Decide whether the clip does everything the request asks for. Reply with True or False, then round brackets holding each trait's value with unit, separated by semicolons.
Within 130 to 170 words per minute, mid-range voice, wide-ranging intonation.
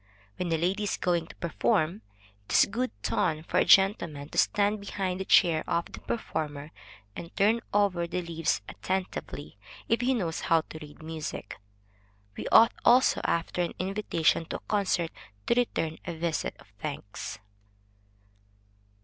False (160 wpm; 170 Hz; 4.0 semitones)